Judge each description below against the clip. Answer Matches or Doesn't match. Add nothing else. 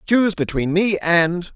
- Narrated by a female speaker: Doesn't match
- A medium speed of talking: Matches